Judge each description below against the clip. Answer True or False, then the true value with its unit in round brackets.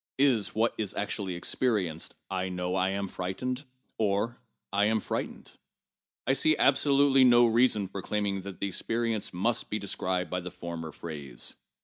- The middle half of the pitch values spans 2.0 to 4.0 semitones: False (4.4 semitones)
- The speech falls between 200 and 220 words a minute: False (160 wpm)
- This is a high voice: False (100 Hz)